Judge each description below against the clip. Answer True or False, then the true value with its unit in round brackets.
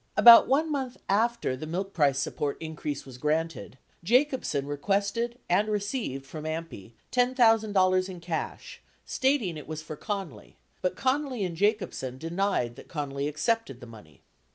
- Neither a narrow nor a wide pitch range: False (7.5 semitones)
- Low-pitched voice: False (180 Hz)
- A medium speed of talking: True (145 wpm)